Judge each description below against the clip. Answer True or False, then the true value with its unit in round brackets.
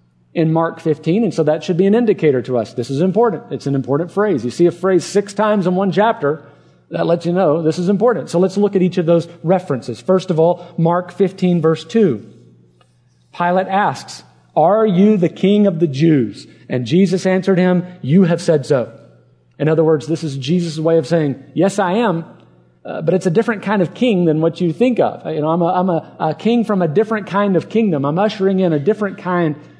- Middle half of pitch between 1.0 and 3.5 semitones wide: False (3.9 semitones)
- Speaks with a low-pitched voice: False (175 Hz)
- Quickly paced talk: True (225 wpm)